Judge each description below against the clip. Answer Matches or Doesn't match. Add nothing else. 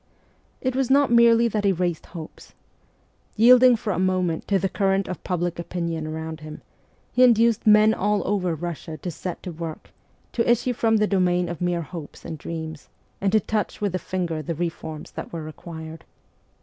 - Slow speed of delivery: Doesn't match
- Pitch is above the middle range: Doesn't match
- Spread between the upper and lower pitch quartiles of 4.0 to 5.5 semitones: Matches